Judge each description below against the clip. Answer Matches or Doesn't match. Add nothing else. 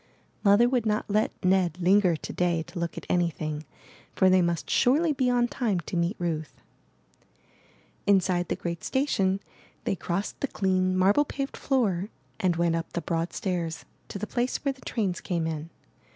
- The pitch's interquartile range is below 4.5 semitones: Matches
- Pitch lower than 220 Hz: Matches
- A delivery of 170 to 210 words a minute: Matches